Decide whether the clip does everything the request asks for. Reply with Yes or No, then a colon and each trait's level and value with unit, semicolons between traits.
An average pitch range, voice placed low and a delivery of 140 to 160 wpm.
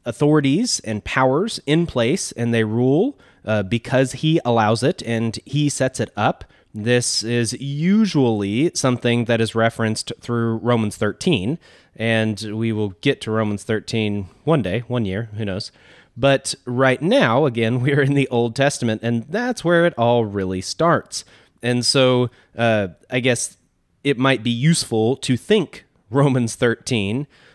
Yes: average, 3.7 semitones; low, 120 Hz; average, 155 wpm